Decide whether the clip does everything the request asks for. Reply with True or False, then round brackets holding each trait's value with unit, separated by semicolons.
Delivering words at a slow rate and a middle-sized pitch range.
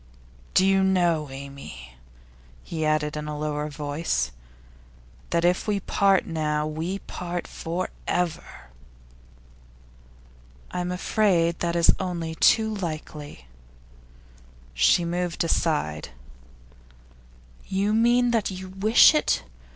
True (105 wpm; 3.9 semitones)